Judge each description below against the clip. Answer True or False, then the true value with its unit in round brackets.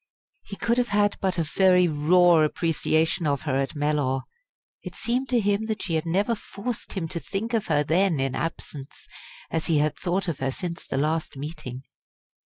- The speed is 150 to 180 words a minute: False (195 wpm)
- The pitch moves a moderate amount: True (5.0 semitones)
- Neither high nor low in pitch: True (165 Hz)